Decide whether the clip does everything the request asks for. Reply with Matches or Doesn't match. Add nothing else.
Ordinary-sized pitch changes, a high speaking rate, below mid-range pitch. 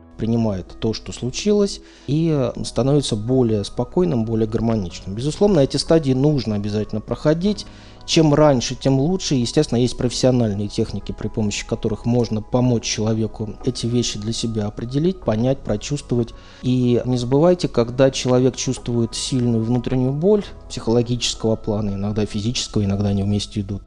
Doesn't match